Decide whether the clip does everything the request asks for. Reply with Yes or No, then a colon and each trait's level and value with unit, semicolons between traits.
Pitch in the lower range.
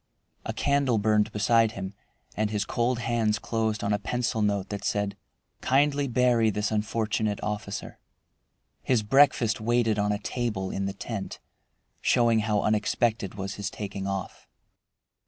Yes: low, 110 Hz